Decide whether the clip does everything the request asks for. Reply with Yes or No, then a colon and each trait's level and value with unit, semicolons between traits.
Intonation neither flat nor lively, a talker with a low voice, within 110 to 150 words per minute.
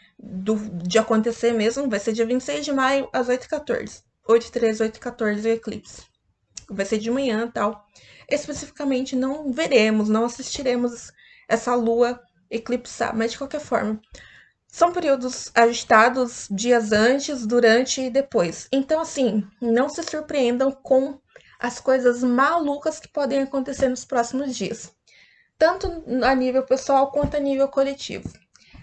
No: average, 3.2 semitones; very high, 250 Hz; average, 130 wpm